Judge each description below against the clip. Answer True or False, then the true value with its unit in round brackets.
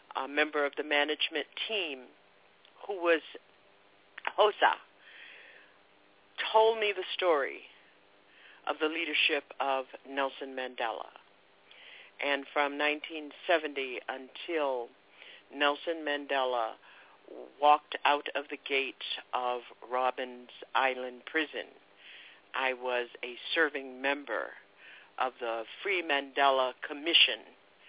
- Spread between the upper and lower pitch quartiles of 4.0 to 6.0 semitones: False (3.2 semitones)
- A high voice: False (135 Hz)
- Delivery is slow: True (95 wpm)